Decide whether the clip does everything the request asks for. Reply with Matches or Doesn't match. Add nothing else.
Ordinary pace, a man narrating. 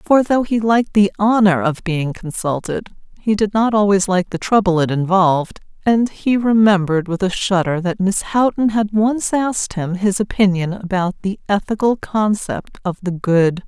Doesn't match